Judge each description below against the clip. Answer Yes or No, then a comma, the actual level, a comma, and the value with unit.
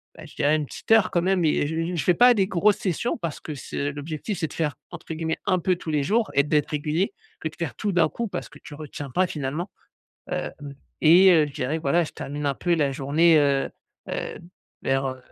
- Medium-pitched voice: Yes, medium, 160 Hz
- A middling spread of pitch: Yes, average, 3.5 semitones